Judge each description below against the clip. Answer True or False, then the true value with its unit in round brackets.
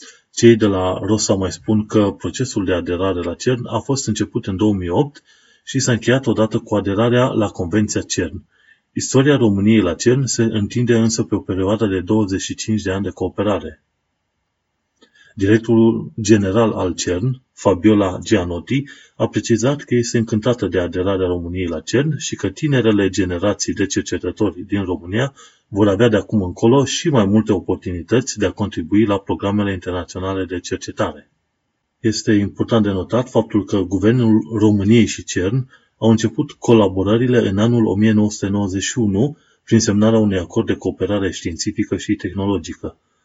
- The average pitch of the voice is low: True (105 Hz)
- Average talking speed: True (150 wpm)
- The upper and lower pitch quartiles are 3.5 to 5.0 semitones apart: False (3.1 semitones)